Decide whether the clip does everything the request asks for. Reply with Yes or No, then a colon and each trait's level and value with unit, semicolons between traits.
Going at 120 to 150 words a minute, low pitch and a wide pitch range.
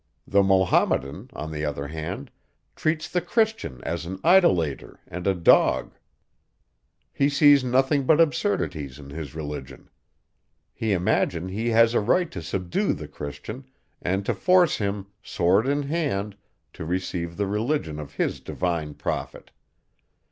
Yes: average, 140 wpm; very low, 95 Hz; wide, 8.7 semitones